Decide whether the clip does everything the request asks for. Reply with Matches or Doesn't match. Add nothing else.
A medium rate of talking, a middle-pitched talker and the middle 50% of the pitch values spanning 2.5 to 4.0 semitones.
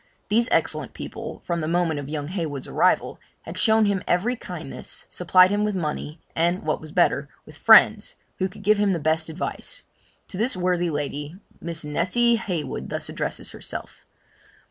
Doesn't match